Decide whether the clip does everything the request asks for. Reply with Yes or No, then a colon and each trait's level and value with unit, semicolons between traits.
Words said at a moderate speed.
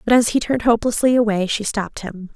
No: fast, 230 wpm